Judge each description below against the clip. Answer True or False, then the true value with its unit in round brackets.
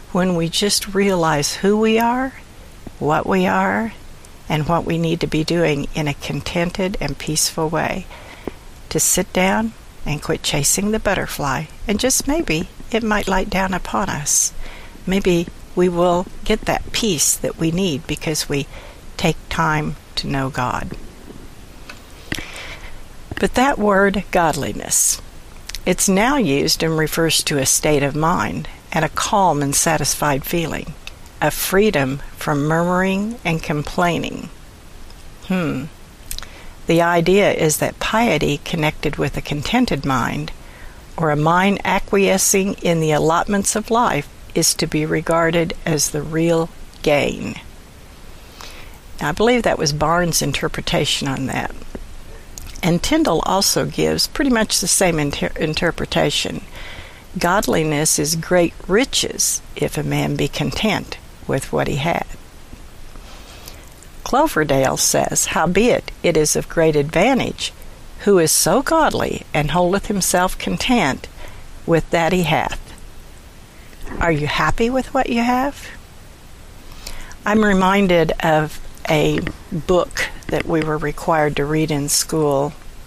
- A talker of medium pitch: True (165 Hz)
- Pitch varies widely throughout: False (4.8 semitones)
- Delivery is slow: True (130 wpm)